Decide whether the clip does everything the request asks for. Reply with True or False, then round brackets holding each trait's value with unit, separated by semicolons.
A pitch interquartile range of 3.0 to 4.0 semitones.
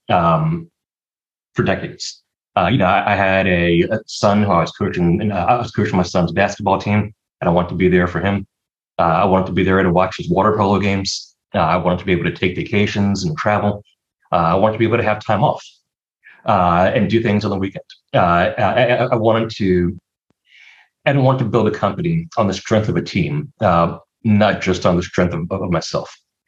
True (3.3 semitones)